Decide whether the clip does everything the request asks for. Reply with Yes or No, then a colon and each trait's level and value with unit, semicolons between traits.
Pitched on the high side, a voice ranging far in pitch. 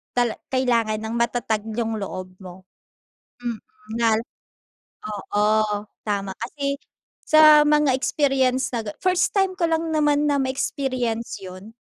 No: high, 240 Hz; average, 4.9 semitones